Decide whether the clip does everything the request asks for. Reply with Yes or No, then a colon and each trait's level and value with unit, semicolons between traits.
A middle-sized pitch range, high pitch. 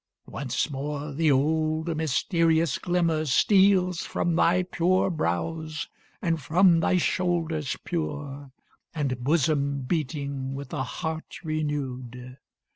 No: average, 3.1 semitones; medium, 155 Hz